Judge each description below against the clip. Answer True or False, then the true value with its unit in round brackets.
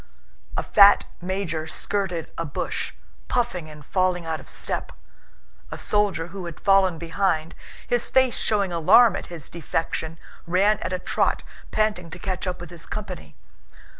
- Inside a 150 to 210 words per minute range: True (155 wpm)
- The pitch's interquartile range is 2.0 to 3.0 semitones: False (3.4 semitones)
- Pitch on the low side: False (180 Hz)